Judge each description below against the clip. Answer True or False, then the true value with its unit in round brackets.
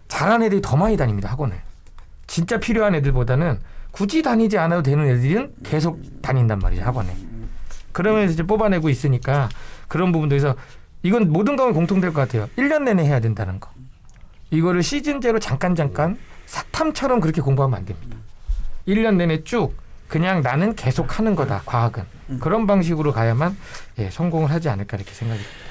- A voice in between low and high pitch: True (145 Hz)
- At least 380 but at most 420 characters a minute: True (385 characters per minute)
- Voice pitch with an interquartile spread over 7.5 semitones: True (8.7 semitones)